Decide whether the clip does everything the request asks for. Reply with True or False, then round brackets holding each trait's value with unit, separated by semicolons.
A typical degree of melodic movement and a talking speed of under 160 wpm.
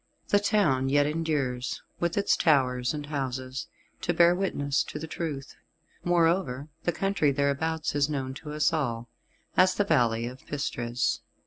True (4.0 semitones; 150 wpm)